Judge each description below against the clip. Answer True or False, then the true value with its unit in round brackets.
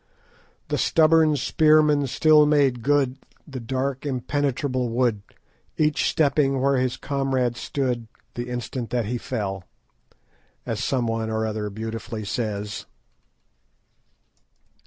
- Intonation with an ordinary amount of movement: True (3.8 semitones)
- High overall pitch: False (130 Hz)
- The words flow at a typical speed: False (110 wpm)